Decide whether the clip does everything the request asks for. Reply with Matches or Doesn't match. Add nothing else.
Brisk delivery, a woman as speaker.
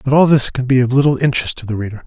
Doesn't match